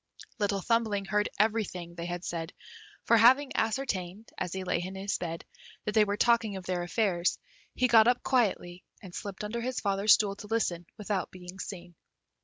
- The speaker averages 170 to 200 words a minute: Yes, average, 185 wpm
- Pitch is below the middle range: No, high, 200 Hz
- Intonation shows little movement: No, average, 3.8 semitones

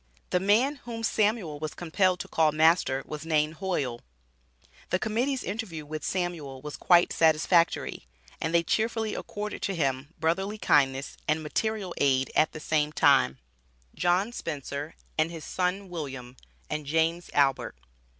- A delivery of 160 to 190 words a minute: No, average, 145 wpm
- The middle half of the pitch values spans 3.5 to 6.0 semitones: Yes, average, 4.4 semitones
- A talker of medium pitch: Yes, medium, 165 Hz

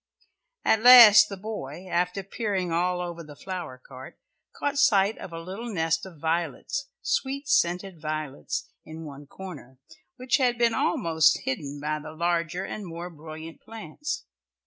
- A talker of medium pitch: Yes, medium, 175 Hz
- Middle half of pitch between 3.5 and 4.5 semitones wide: No, average, 5.1 semitones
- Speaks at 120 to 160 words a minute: Yes, average, 150 wpm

